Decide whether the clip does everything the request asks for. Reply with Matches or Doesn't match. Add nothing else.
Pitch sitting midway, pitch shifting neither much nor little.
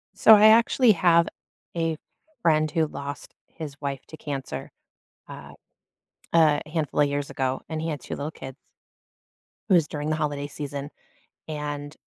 Doesn't match